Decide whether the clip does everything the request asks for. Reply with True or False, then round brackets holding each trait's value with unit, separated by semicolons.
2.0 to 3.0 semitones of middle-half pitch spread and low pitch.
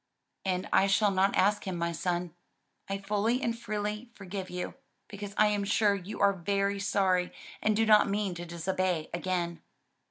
False (2.4 semitones; 195 Hz)